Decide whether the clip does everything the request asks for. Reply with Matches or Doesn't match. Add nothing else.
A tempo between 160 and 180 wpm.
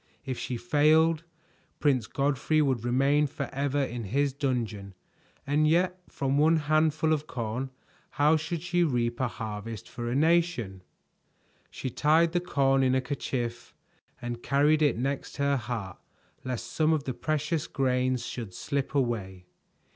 Doesn't match